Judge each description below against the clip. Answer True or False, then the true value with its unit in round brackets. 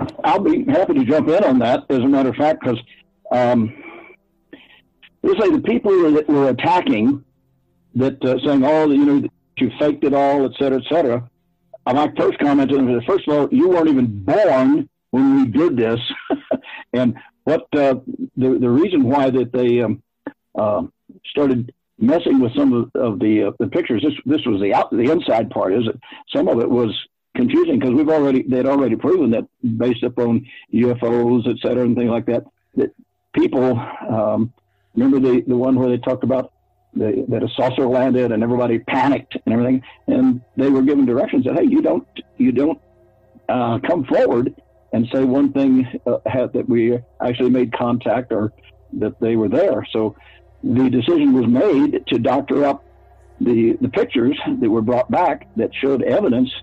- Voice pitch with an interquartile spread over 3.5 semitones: False (3.1 semitones)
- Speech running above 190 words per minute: False (185 wpm)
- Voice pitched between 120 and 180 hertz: True (130 Hz)